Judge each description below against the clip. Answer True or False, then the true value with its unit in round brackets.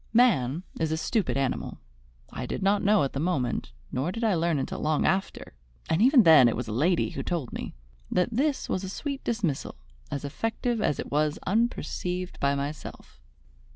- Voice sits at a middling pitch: True (170 Hz)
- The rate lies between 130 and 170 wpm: False (190 wpm)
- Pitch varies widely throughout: True (7.2 semitones)